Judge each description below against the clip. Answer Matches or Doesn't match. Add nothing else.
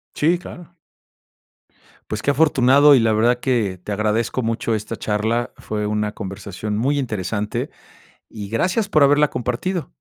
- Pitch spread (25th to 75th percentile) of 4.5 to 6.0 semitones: Matches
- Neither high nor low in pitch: Doesn't match